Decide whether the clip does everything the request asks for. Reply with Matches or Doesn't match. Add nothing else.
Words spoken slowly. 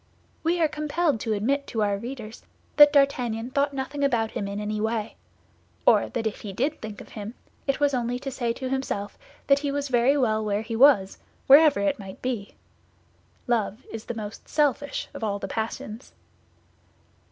Doesn't match